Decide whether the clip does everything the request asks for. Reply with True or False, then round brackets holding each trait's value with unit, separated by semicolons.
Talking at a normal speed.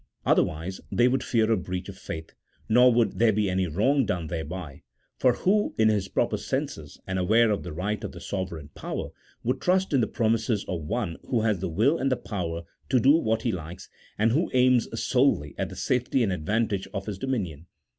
False (210 wpm)